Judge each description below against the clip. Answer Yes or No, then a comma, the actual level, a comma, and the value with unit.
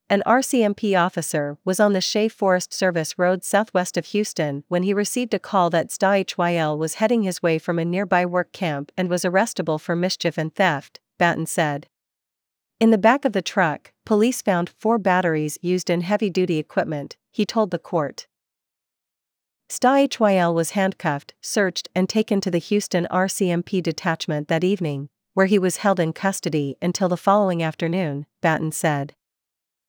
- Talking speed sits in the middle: Yes, average, 170 wpm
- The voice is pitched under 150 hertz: No, medium, 180 Hz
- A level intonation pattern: No, average, 3.5 semitones